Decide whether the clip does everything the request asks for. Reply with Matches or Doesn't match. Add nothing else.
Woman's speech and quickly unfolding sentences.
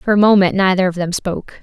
Matches